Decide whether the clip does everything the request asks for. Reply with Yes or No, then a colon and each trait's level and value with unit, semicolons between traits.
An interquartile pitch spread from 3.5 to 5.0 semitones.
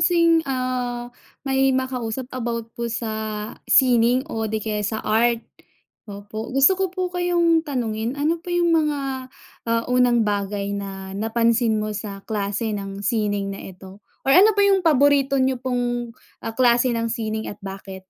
Yes: average, 4.0 semitones